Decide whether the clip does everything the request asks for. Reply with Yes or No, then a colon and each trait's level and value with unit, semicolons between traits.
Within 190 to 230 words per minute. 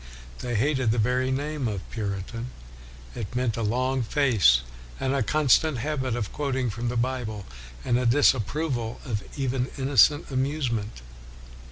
No: average, 150 wpm